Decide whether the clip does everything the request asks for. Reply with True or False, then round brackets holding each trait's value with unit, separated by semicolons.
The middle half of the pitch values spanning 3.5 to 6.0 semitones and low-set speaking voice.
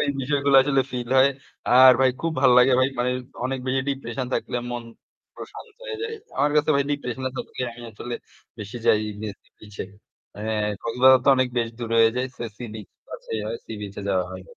False (3.1 semitones; 125 Hz)